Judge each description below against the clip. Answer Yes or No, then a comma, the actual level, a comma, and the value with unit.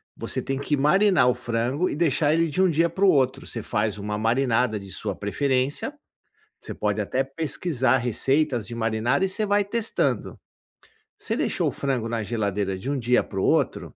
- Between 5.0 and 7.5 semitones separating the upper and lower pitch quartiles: Yes, wide, 5.5 semitones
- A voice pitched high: No, low, 130 Hz